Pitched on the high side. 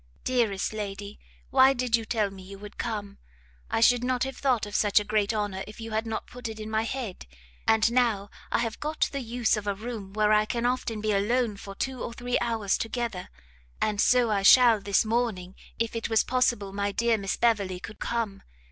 Yes: high, 220 Hz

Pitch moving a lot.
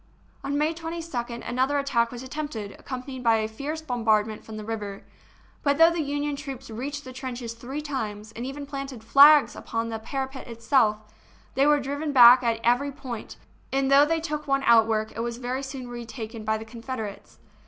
No: average, 3.8 semitones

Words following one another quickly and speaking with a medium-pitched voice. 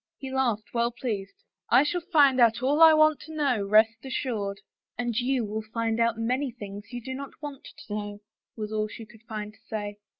No: fast, 220 wpm; high, 230 Hz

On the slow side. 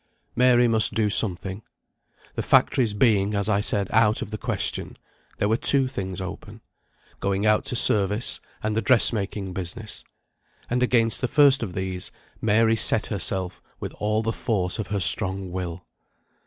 No: average, 160 wpm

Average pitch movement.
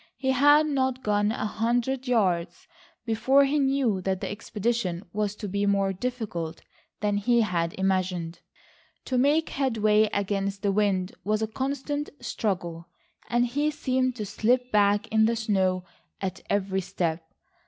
Yes: average, 4.7 semitones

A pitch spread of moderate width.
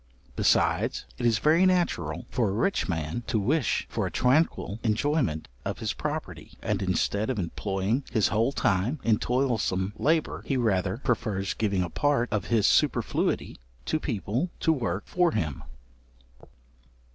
No: wide, 6.0 semitones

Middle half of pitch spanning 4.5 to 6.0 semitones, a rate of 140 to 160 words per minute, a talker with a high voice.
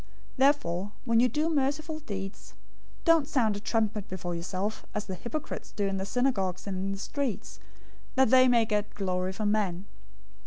No: average, 5.3 semitones; average, 180 wpm; high, 210 Hz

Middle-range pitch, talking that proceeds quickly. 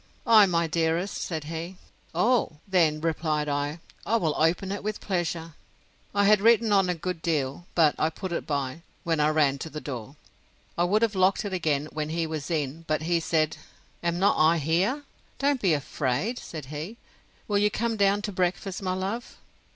No: medium, 170 Hz; average, 190 wpm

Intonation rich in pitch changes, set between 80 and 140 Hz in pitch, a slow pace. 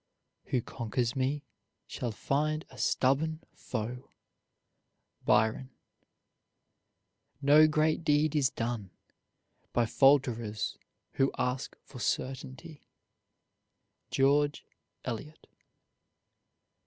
No: average, 3.5 semitones; low, 135 Hz; slow, 80 wpm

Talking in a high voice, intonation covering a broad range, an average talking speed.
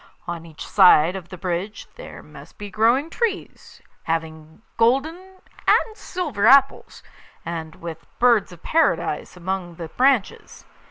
No: high, 195 Hz; wide, 8.3 semitones; slow, 130 wpm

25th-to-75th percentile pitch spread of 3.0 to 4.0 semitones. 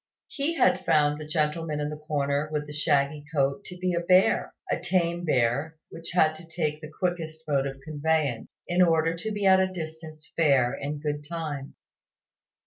No: narrow, 2.5 semitones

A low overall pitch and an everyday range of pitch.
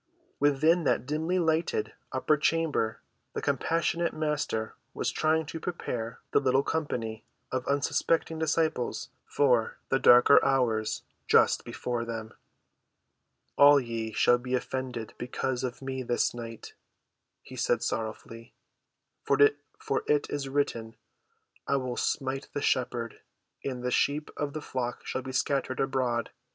Yes: low, 130 Hz; average, 3.6 semitones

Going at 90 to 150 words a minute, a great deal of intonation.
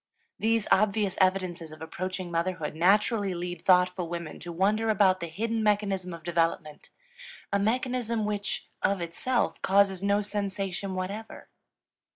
No: slow, 135 wpm; average, 3.1 semitones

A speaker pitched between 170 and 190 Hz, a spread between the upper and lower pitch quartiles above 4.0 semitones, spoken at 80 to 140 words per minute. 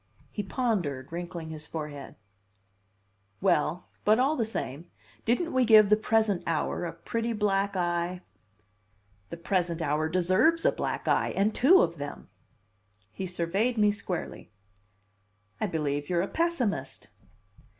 Yes: medium, 185 Hz; average, 4.9 semitones; slow, 135 wpm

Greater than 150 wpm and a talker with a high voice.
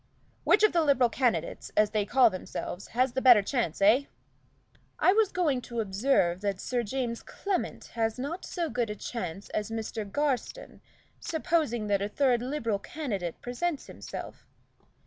Yes: average, 160 wpm; high, 240 Hz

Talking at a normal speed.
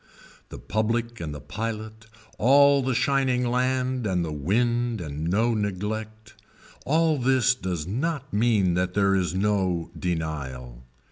No: slow, 130 wpm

